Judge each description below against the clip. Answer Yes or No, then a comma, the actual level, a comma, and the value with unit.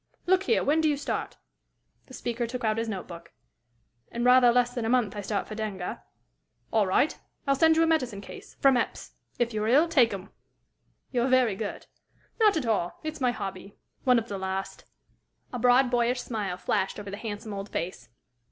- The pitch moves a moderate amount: Yes, average, 4.1 semitones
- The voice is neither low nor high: No, high, 235 Hz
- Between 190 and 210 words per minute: Yes, average, 200 wpm